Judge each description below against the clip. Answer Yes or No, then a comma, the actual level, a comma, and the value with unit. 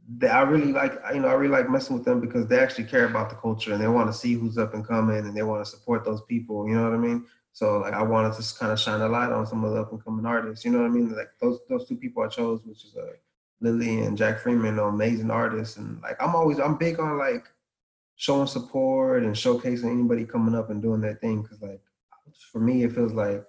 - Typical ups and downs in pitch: No, wide, 6.0 semitones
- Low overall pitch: Yes, low, 115 Hz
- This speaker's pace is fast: Yes, fast, 275 wpm